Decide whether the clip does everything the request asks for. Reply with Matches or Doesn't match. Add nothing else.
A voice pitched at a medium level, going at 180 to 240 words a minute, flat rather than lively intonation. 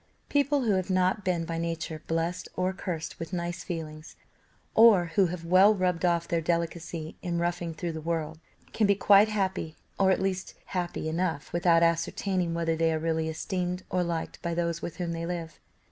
Matches